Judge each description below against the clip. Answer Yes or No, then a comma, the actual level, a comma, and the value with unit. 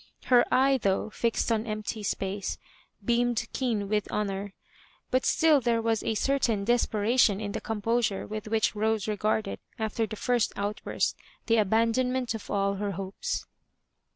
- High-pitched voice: Yes, high, 220 Hz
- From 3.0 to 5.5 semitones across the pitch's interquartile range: No, narrow, 2.6 semitones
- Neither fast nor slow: Yes, average, 145 wpm